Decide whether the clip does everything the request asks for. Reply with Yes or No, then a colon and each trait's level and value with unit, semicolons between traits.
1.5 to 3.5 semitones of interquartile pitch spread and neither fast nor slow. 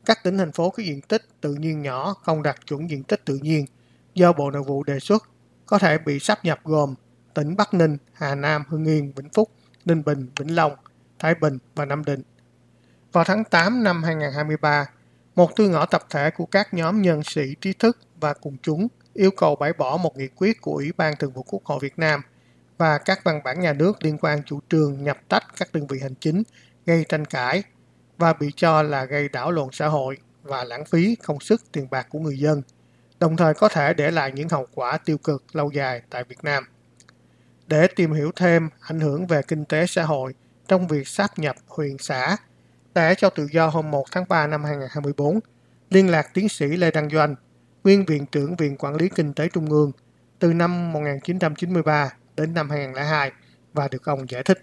Yes: average, 3.1 semitones; average, 210 wpm